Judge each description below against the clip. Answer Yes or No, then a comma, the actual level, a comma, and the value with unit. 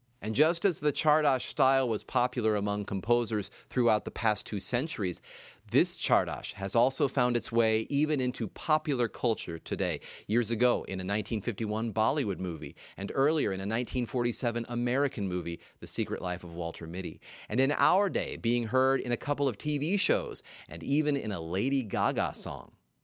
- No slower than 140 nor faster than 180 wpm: Yes, average, 170 wpm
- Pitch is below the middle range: Yes, low, 120 Hz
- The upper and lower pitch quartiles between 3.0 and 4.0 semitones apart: No, average, 4.5 semitones